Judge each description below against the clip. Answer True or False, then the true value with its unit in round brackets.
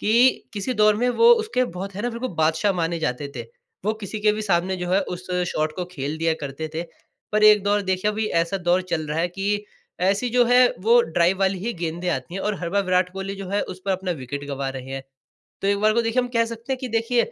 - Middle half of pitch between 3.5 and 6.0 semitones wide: True (4.0 semitones)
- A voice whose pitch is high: True (195 Hz)